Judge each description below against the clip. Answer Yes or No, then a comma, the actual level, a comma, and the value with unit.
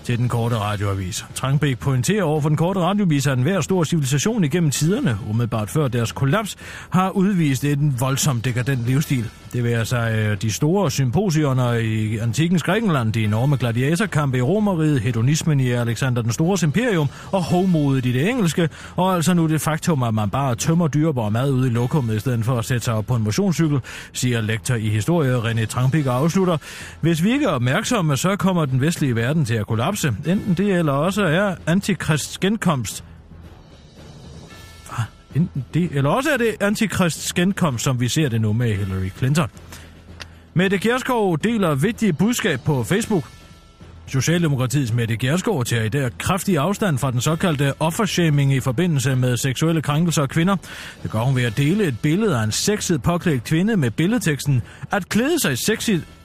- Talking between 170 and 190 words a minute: Yes, average, 175 wpm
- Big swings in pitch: Yes, wide, 6.7 semitones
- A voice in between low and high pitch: Yes, medium, 145 Hz